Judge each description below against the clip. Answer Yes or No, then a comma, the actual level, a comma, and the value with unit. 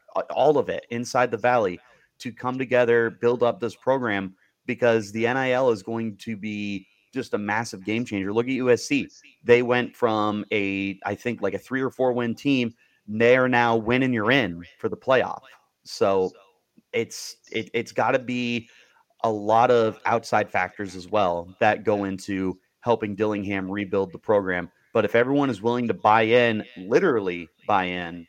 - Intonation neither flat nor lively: Yes, average, 3.5 semitones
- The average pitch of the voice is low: Yes, low, 115 Hz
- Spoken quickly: No, average, 180 wpm